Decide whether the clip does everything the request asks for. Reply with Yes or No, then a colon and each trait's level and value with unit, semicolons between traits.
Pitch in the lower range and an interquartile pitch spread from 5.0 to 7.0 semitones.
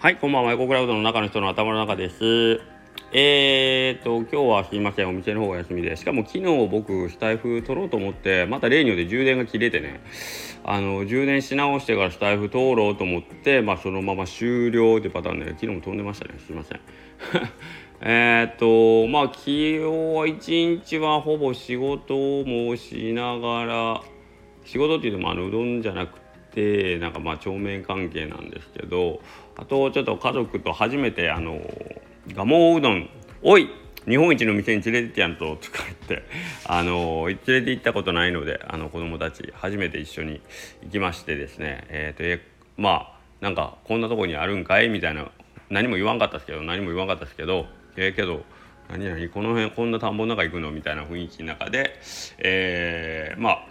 Yes: low, 105 Hz; wide, 5.6 semitones